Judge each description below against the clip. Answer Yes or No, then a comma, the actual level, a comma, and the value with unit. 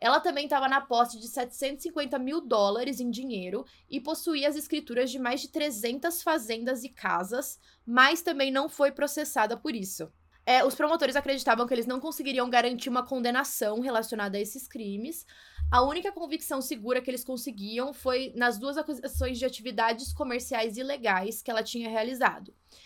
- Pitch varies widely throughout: No, average, 3.3 semitones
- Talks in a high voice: Yes, very high, 255 Hz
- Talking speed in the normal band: Yes, average, 165 wpm